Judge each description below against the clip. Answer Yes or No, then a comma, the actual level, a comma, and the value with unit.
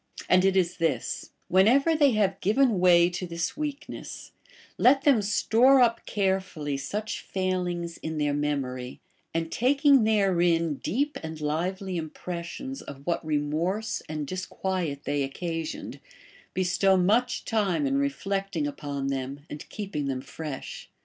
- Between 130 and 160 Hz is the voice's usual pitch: No, medium, 180 Hz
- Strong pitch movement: Yes, wide, 5.7 semitones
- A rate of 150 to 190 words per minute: No, slow, 135 wpm